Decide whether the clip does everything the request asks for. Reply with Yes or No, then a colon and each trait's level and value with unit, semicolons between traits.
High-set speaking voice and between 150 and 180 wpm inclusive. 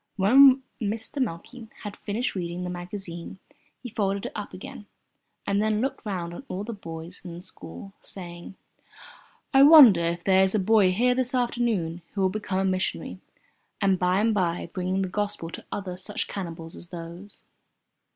Yes: high, 195 Hz; average, 175 wpm